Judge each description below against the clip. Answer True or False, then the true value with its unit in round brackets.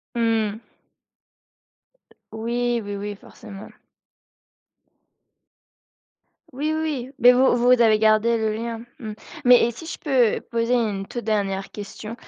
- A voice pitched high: True (230 Hz)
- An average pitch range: False (2.2 semitones)